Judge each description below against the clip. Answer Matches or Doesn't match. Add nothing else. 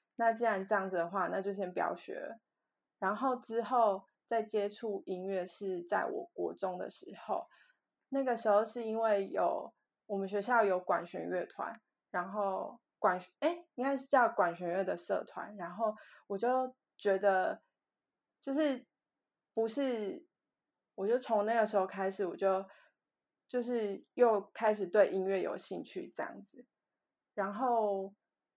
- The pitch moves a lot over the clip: Doesn't match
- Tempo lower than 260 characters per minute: Matches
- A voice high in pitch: Matches